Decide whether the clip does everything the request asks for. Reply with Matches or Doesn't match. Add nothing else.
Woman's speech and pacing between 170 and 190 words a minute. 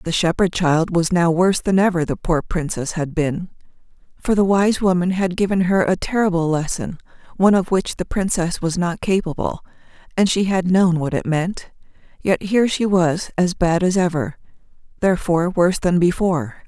Matches